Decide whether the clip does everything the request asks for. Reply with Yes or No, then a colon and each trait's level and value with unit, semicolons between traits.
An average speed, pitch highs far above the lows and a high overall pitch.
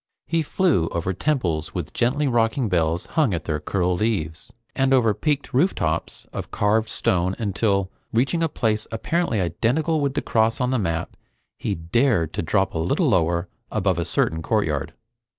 No: average, 170 wpm; wide, 7.3 semitones; low, 105 Hz